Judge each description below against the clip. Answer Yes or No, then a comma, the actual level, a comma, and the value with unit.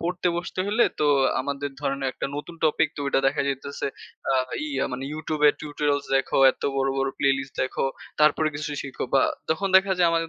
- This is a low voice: No, medium, 150 Hz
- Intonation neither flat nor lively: Yes, average, 3.3 semitones